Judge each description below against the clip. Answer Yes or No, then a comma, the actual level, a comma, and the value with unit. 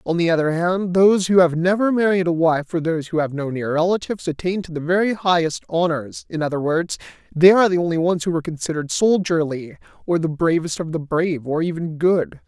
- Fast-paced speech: Yes, fast, 215 wpm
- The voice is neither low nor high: Yes, medium, 170 Hz